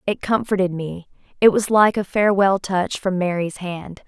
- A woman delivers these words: Yes, female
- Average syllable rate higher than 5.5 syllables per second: No, 4.7 syllables/s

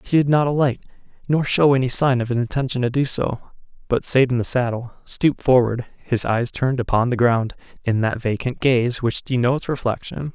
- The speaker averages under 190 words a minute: No, average, 195 wpm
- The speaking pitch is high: No, low, 125 Hz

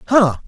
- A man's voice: Yes, male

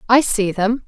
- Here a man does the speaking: No, female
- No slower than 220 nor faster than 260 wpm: No, fast, 205 wpm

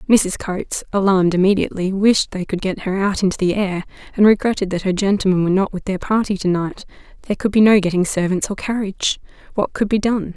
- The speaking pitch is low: No, high, 195 Hz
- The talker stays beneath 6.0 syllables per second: No, 6.3 syllables/s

